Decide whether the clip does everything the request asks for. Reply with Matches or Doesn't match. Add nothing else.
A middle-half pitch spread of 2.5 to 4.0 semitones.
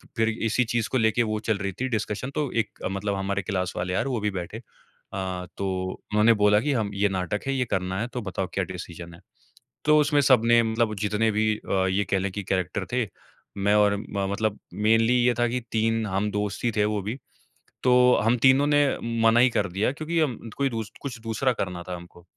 Matches